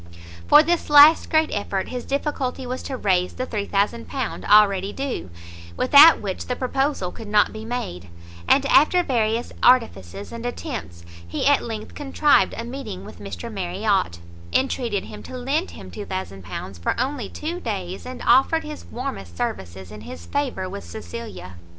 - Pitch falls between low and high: No, high, 225 Hz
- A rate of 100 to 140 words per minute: No, average, 155 wpm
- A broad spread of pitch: Yes, wide, 6.4 semitones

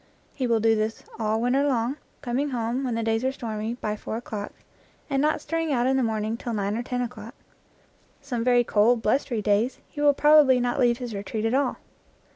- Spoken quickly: Yes, fast, 220 wpm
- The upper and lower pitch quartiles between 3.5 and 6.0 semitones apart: No, average, 2.9 semitones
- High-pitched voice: Yes, high, 240 Hz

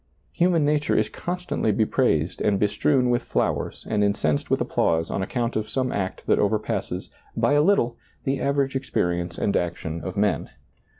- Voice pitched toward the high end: No, low, 115 Hz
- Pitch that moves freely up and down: Yes, wide, 6.9 semitones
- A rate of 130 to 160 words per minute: No, average, 175 wpm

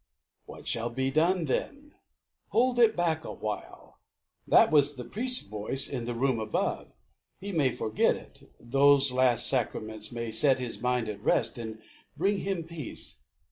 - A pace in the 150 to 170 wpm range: Yes, average, 155 wpm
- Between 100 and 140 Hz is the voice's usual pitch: Yes, low, 135 Hz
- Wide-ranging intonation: Yes, wide, 6.1 semitones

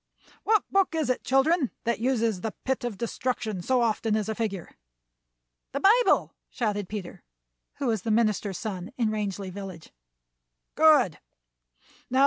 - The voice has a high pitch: Yes, high, 225 Hz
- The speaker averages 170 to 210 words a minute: No, average, 140 wpm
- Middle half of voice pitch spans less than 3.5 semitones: No, average, 4.2 semitones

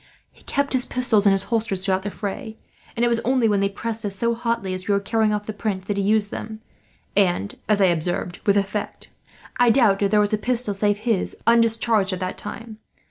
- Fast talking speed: Yes, fast, 230 wpm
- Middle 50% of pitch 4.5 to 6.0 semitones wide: No, narrow, 2.6 semitones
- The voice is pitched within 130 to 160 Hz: No, high, 210 Hz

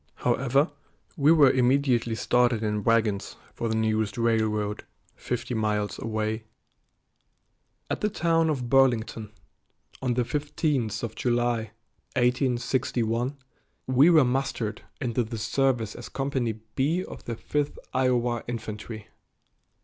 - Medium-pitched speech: No, low, 120 Hz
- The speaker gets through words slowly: Yes, slow, 120 wpm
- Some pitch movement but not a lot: Yes, average, 3.3 semitones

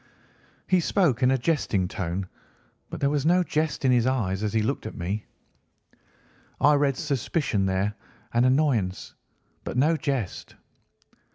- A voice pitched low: Yes, low, 130 Hz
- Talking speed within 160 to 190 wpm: No, average, 150 wpm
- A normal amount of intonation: No, wide, 6.1 semitones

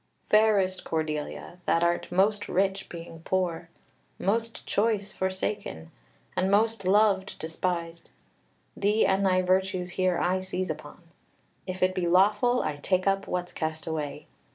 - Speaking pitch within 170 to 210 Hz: Yes, medium, 185 Hz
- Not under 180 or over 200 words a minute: No, slow, 135 wpm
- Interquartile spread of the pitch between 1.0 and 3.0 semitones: Yes, narrow, 2.4 semitones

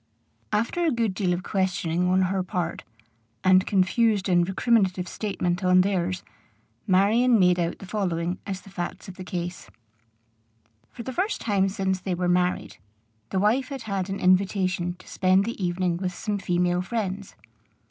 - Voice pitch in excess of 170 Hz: Yes, medium, 185 Hz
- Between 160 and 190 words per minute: Yes, average, 165 wpm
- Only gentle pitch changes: Yes, narrow, 2.1 semitones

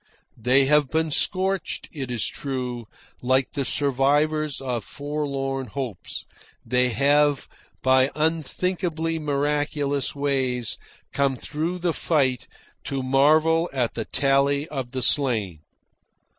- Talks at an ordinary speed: No, slow, 115 wpm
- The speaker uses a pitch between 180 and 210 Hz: No, medium, 140 Hz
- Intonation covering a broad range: No, average, 2.7 semitones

